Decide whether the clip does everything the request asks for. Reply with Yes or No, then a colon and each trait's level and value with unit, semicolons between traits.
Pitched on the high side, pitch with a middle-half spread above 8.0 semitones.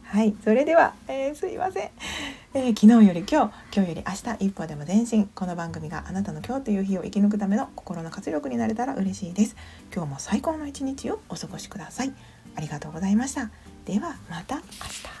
No: high, 210 Hz; wide, 5.5 semitones